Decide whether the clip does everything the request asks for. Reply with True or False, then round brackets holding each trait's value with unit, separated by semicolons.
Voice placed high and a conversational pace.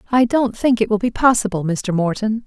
False (220 Hz; 220 wpm)